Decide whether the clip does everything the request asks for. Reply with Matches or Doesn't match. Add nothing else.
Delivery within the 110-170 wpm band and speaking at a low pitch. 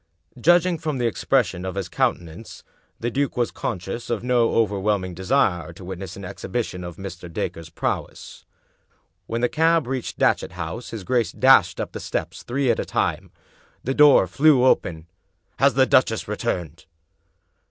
Matches